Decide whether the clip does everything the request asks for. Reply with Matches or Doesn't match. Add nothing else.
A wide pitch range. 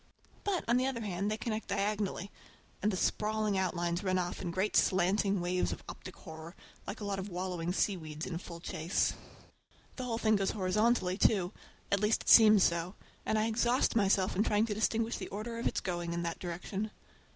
Doesn't match